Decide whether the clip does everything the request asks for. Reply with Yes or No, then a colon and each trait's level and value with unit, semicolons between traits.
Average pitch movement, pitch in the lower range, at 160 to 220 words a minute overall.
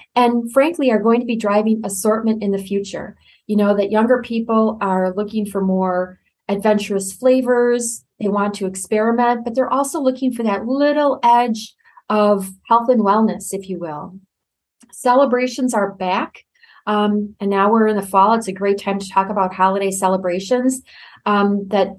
No: average, 3.5 semitones; high, 210 Hz; average, 170 wpm